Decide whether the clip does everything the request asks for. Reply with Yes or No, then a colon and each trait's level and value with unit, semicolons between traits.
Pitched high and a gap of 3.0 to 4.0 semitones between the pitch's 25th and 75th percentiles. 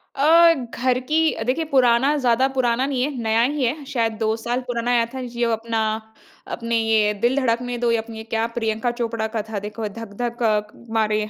No: high, 235 Hz; narrow, 2.4 semitones